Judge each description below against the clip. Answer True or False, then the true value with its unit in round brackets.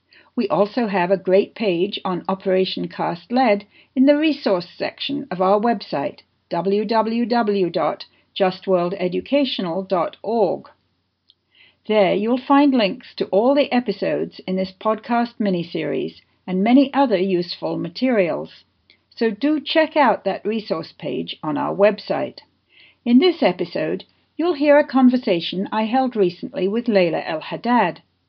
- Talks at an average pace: False (125 wpm)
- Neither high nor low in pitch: False (205 Hz)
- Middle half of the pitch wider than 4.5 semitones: True (5.1 semitones)